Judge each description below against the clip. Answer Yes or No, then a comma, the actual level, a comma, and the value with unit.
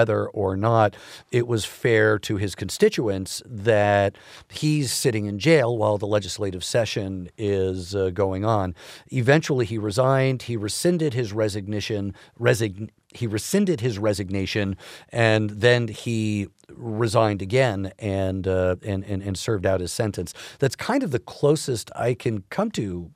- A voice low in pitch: Yes, low, 110 Hz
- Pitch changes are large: No, average, 3.5 semitones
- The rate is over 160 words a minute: No, average, 150 wpm